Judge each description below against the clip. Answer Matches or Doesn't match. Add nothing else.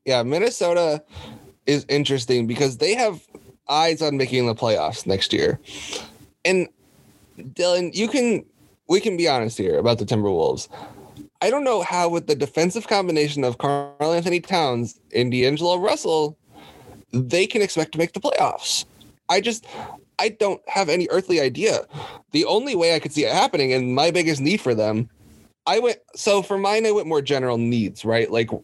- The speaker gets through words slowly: Doesn't match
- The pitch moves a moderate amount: Doesn't match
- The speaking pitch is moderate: Matches